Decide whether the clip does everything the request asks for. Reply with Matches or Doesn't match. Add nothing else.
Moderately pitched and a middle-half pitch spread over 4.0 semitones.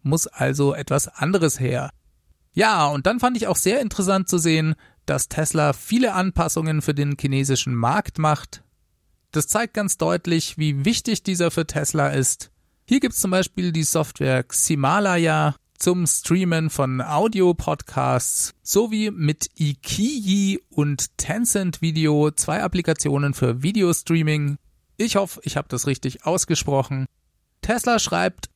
Matches